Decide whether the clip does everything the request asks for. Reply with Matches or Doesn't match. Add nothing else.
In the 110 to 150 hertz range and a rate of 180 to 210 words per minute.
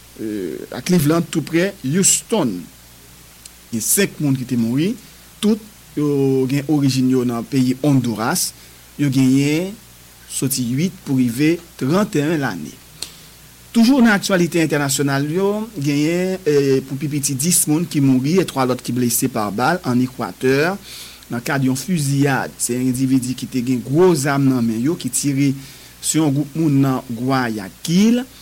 Doesn't match